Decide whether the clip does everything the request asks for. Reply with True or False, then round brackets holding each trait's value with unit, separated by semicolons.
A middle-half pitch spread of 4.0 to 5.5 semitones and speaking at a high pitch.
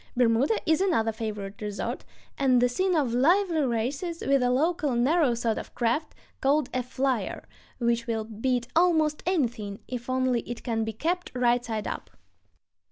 True (4.8 semitones; 250 Hz)